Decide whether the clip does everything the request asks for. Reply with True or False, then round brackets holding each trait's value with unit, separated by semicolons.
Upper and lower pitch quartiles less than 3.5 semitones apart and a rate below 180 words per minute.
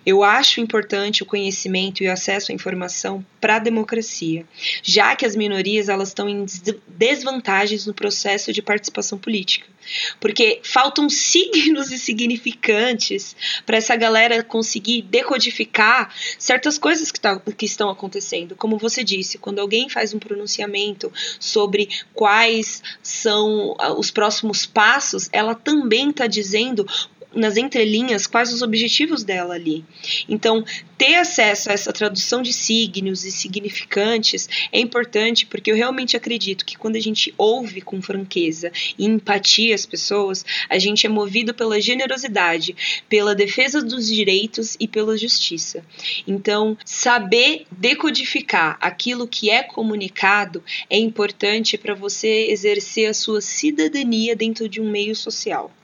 True (2.8 semitones; 140 wpm)